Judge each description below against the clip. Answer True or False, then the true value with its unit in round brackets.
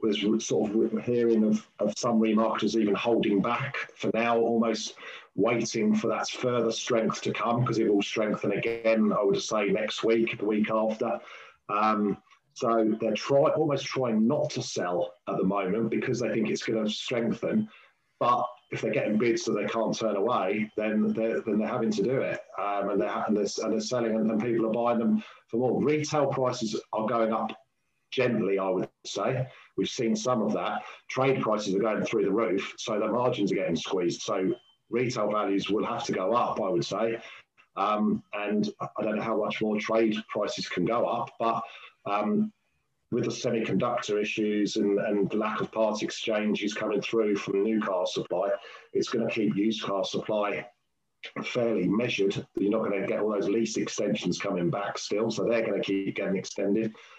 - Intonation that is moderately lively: False (1.6 semitones)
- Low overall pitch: True (110 Hz)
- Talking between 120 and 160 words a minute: False (195 wpm)